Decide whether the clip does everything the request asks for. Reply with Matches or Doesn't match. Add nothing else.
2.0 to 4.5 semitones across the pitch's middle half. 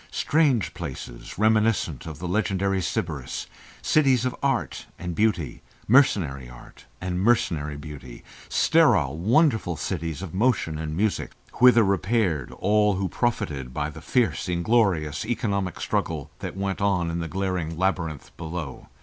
Doesn't match